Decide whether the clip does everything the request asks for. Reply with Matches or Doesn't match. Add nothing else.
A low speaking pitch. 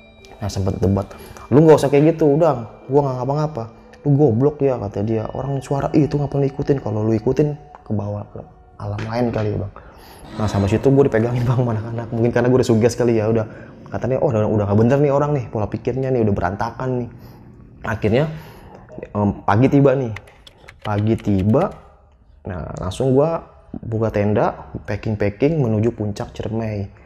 Matches